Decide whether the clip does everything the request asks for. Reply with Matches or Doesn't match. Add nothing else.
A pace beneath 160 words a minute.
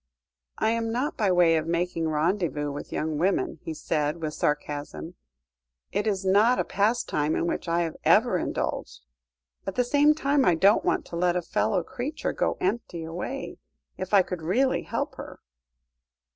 Doesn't match